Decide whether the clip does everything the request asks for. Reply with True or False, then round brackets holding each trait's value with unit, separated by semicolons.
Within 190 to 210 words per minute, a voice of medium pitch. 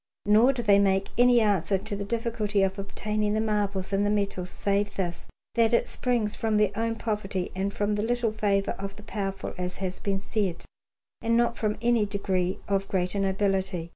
False (195 wpm; 205 Hz)